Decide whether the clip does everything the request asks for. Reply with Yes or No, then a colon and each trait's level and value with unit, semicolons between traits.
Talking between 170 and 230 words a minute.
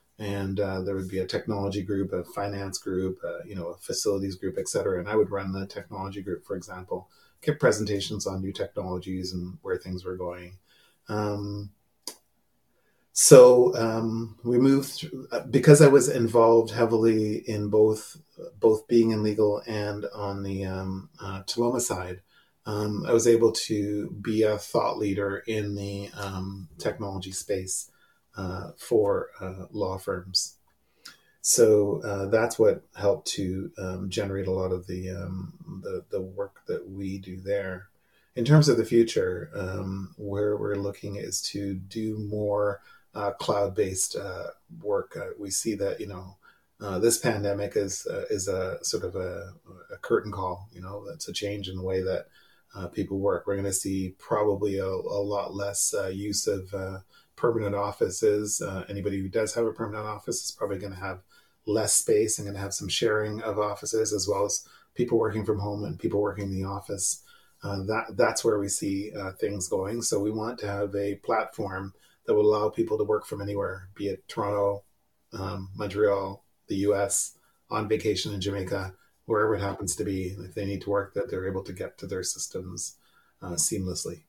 Yes: average, 180 wpm